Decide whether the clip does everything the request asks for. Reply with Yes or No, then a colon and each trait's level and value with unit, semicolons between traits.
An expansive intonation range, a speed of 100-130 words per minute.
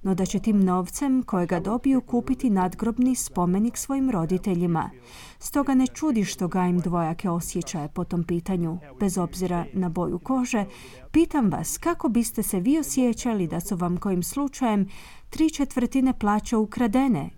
No: wide, 6.1 semitones; average, 150 wpm